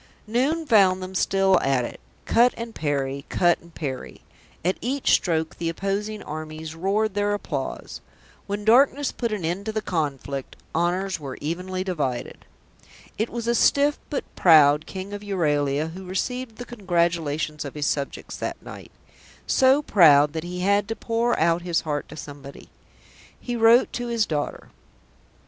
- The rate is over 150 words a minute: Yes, average, 160 wpm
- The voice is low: No, medium, 185 Hz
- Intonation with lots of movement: Yes, wide, 6.0 semitones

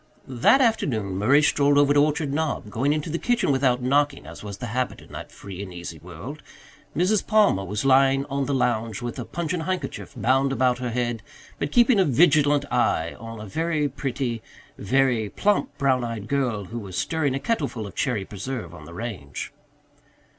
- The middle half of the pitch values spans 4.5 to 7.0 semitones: Yes, average, 4.9 semitones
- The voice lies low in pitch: Yes, low, 130 Hz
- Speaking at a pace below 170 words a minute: No, average, 190 wpm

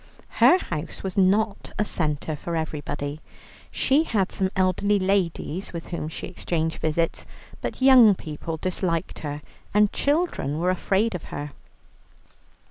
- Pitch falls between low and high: Yes, medium, 180 Hz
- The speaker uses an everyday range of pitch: Yes, average, 4.3 semitones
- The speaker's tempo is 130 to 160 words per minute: Yes, slow, 135 wpm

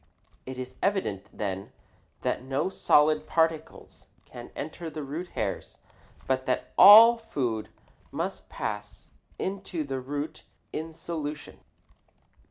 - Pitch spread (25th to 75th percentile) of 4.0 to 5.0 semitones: Yes, average, 4.4 semitones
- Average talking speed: No, slow, 115 wpm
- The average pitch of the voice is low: No, medium, 150 Hz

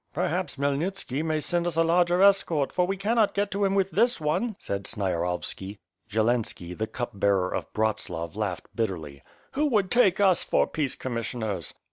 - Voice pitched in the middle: Yes, medium, 150 Hz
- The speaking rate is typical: Yes, average, 170 wpm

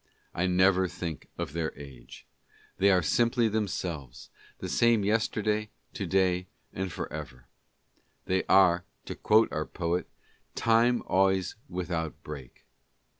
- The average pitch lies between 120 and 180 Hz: No, very low, 90 Hz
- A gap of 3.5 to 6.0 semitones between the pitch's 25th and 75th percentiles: Yes, average, 4.1 semitones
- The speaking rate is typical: No, slow, 130 wpm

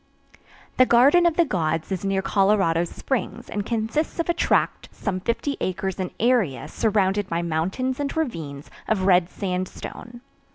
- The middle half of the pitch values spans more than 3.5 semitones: Yes, average, 5.3 semitones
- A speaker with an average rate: Yes, average, 155 wpm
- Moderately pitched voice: No, high, 200 Hz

